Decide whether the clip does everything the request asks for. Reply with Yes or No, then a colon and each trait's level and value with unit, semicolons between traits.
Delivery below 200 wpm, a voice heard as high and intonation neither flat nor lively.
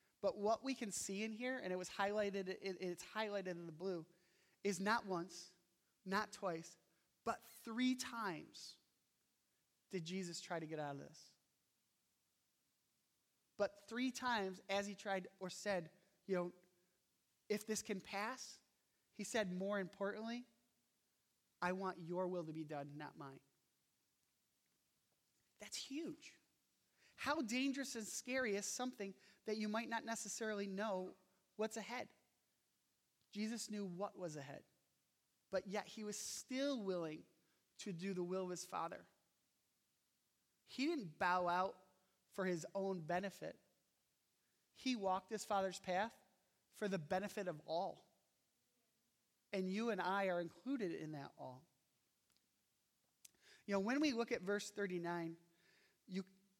Yes: slow, 135 wpm; high, 195 Hz; average, 3.2 semitones